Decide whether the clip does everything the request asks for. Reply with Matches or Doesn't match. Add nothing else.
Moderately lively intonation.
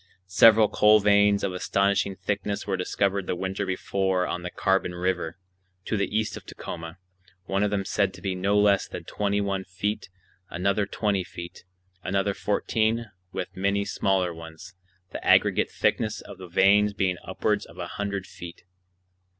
Doesn't match